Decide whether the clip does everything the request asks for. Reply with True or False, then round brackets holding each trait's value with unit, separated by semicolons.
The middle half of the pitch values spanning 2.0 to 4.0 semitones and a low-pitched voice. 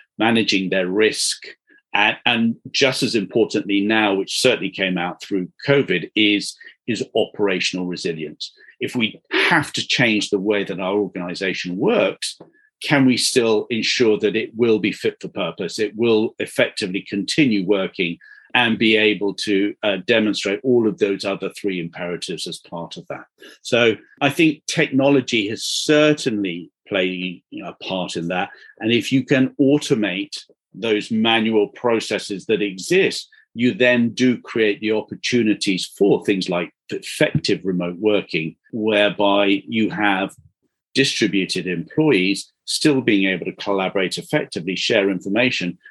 False (4.4 semitones; 105 Hz)